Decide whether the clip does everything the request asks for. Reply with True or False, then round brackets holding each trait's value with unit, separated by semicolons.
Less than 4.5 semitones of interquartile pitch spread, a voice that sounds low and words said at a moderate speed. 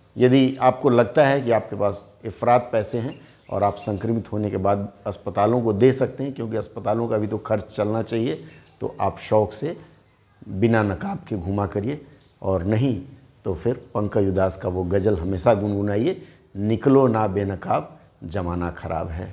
True (3.1 semitones; 110 Hz; 170 wpm)